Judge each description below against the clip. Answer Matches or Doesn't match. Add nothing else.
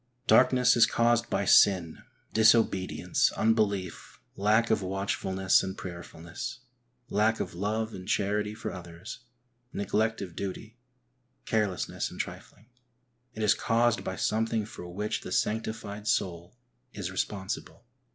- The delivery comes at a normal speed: Doesn't match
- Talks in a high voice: Doesn't match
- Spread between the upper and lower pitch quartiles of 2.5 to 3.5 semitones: Matches